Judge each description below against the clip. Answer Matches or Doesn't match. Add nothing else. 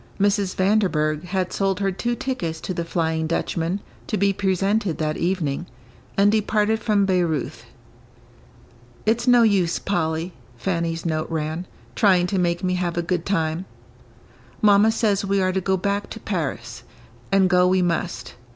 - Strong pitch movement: Doesn't match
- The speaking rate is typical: Matches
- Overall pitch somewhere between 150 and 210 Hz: Matches